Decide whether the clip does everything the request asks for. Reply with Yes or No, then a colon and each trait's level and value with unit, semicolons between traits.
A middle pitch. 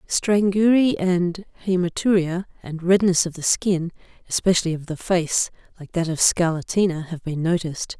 Yes: medium, 175 Hz